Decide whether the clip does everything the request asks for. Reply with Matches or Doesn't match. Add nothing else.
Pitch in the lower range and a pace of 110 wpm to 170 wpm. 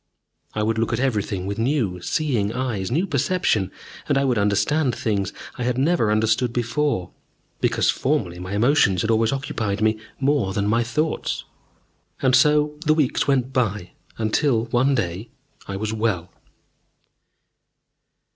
Matches